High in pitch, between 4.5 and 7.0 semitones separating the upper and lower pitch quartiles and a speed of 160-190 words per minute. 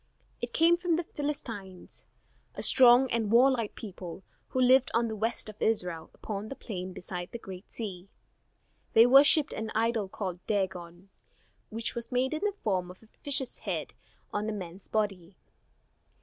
Yes: high, 220 Hz; average, 4.9 semitones; average, 165 wpm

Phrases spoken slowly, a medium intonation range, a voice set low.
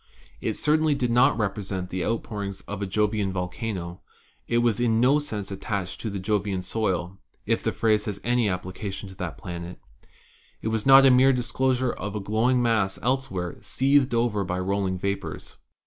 No: average, 190 wpm; average, 4.1 semitones; low, 105 Hz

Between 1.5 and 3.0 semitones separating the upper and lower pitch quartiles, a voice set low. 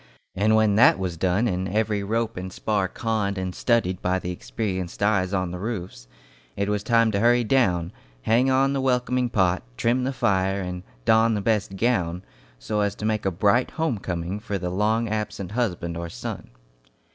No: average, 3.6 semitones; low, 100 Hz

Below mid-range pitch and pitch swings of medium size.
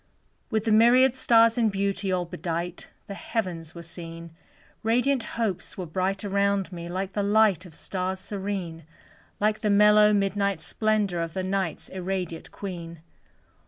No: high, 195 Hz; average, 3.2 semitones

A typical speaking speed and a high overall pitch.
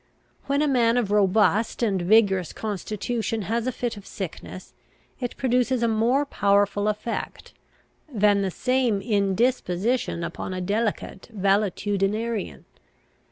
No: slow, 120 wpm; high, 215 Hz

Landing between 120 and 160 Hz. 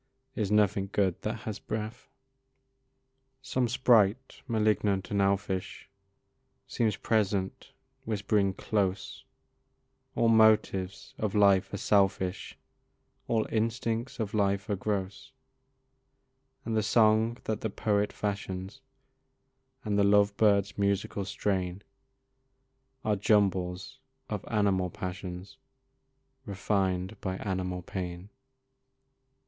No: low, 100 Hz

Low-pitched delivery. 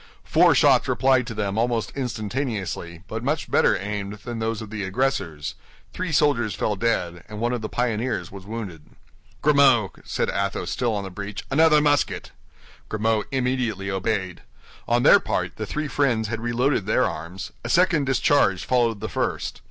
Yes: low, 115 Hz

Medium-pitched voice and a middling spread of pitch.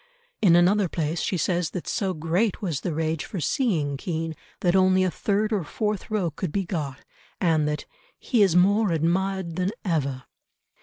Yes: medium, 175 Hz; average, 3.3 semitones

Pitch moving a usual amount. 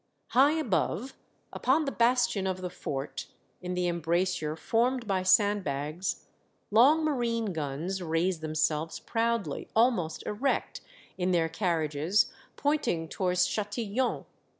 No: wide, 6.1 semitones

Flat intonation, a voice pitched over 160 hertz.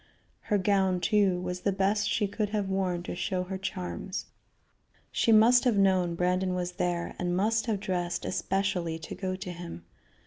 Yes: narrow, 2.1 semitones; high, 190 Hz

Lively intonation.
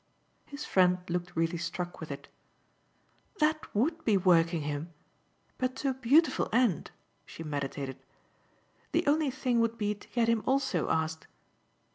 Yes: wide, 7.8 semitones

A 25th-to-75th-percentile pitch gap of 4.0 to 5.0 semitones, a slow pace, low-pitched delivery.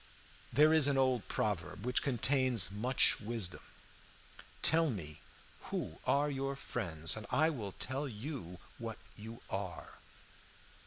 No: wide, 5.4 semitones; slow, 125 wpm; low, 120 Hz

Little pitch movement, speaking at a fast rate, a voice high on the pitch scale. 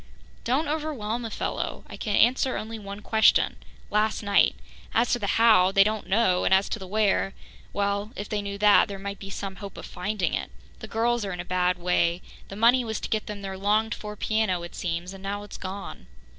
Yes: narrow, 2.3 semitones; fast, 220 wpm; high, 205 Hz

